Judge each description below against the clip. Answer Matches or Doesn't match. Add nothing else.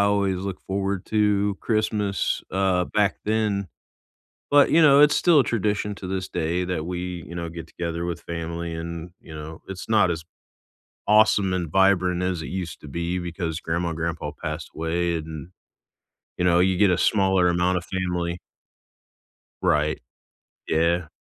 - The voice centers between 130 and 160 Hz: Doesn't match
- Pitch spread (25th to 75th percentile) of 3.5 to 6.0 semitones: Doesn't match